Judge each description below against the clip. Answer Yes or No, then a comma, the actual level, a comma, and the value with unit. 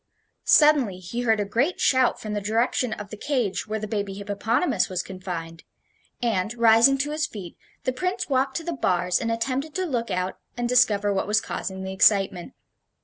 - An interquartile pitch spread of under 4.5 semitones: No, average, 4.9 semitones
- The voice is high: Yes, high, 220 Hz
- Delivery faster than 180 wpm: Yes, average, 190 wpm